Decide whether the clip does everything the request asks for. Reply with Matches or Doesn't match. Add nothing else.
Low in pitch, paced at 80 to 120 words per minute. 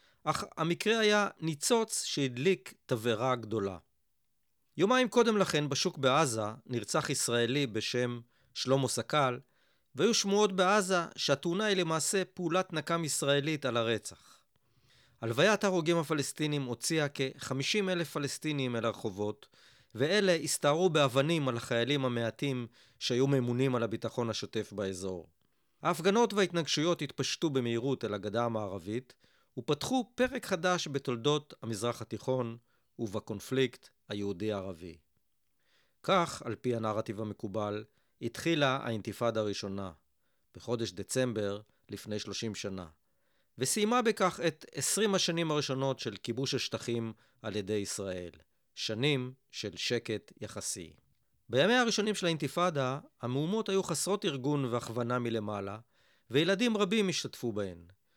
Matches